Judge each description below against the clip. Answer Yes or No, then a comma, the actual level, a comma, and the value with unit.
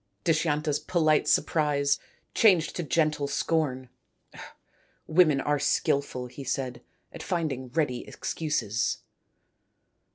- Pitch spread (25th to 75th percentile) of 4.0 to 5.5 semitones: No, average, 2.8 semitones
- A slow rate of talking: Yes, slow, 105 wpm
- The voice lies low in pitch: No, medium, 150 Hz